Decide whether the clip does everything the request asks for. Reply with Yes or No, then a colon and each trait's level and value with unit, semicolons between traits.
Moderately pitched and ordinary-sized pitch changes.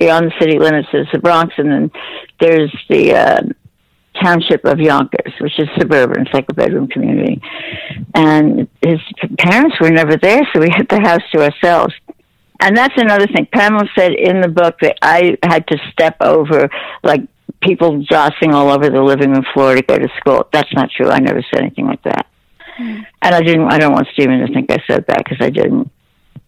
Yes: medium, 165 Hz; average, 3.7 semitones